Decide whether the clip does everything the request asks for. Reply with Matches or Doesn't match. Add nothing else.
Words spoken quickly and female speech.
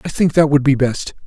Doesn't match